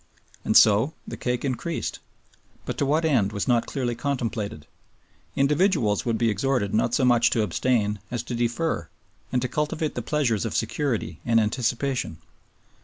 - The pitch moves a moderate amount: Yes, average, 3.9 semitones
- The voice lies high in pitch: No, low, 120 Hz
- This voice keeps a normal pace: Yes, average, 160 wpm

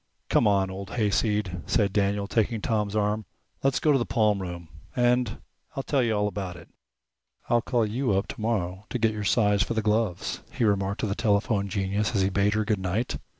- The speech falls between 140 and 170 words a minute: No, average, 200 wpm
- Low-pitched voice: Yes, low, 105 Hz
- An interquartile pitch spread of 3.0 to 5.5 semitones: No, narrow, 2.4 semitones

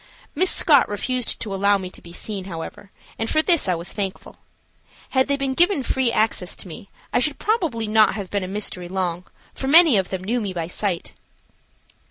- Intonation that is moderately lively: No, wide, 6.0 semitones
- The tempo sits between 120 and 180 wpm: No, fast, 205 wpm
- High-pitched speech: Yes, high, 210 Hz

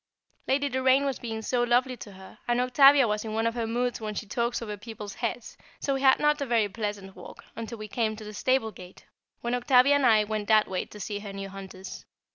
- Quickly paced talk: Yes, fast, 240 wpm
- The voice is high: Yes, high, 225 Hz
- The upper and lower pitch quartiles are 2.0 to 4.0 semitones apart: Yes, average, 3.1 semitones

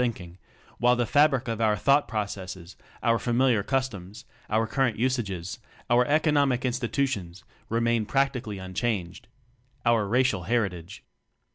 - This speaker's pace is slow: Yes, slow, 120 wpm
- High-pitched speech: No, low, 115 Hz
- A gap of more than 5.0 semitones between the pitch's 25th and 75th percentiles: No, average, 4.4 semitones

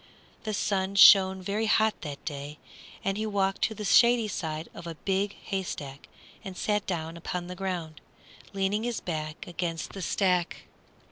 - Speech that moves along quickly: No, average, 160 wpm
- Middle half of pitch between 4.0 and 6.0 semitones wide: No, average, 3.4 semitones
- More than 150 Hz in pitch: Yes, high, 190 Hz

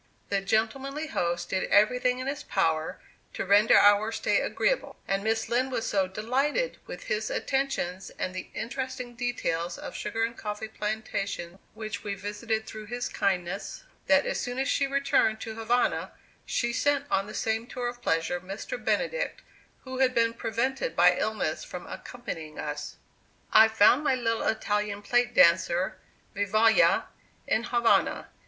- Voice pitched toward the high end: Yes, high, 220 Hz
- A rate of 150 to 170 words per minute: Yes, average, 155 wpm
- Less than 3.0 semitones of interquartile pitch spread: No, average, 3.8 semitones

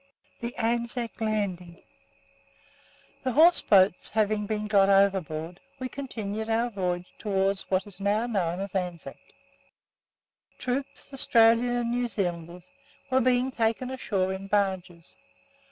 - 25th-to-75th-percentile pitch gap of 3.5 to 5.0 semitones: Yes, average, 3.9 semitones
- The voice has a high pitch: Yes, high, 210 Hz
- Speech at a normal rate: No, slow, 120 wpm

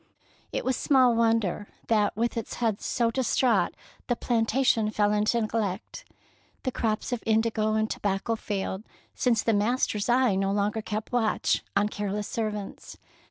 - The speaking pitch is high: Yes, high, 220 Hz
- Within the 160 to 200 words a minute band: No, average, 150 wpm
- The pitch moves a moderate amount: No, narrow, 2.1 semitones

